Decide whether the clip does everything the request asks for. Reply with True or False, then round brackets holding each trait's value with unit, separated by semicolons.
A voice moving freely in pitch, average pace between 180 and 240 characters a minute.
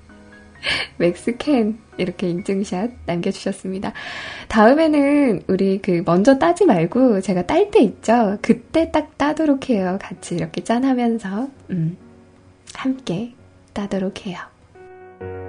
True (7.1 semitones; 230 characters per minute)